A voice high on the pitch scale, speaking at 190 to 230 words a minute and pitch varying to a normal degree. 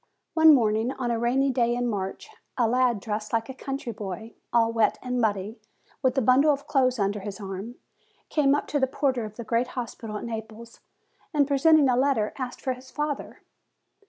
Yes: high, 240 Hz; average, 195 wpm; average, 3.4 semitones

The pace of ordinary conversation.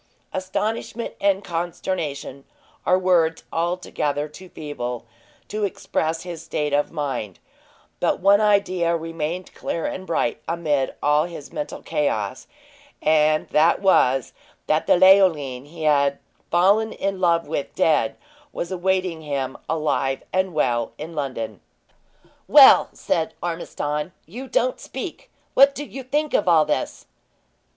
No: slow, 130 wpm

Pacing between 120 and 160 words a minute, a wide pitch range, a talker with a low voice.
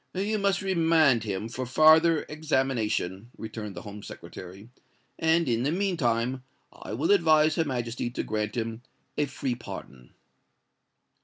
Yes: average, 145 wpm; wide, 6.3 semitones; low, 130 Hz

